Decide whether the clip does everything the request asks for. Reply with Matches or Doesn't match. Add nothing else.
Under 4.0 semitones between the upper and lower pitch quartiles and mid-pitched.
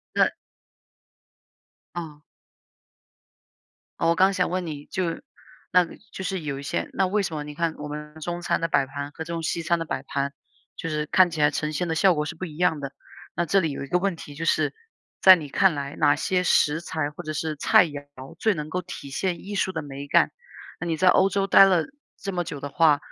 Matches